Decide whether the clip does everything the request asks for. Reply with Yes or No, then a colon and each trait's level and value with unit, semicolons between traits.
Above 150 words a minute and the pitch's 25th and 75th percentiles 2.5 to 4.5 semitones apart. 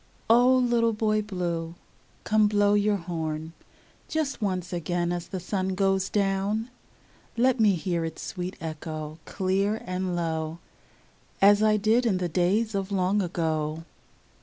No: average, 140 wpm; average, 3.7 semitones